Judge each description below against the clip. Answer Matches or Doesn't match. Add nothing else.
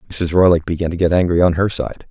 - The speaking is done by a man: Matches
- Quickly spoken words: Matches